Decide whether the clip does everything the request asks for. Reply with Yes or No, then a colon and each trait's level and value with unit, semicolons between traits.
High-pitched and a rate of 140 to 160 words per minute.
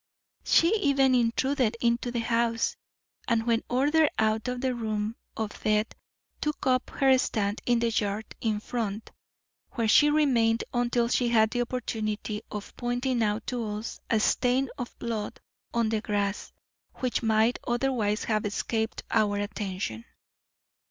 Yes: high, 230 Hz; average, 145 wpm